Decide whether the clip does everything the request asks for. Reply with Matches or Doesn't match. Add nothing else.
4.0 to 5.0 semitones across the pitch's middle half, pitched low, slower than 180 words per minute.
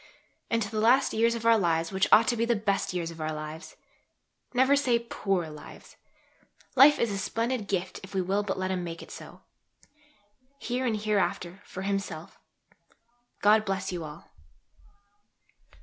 Doesn't match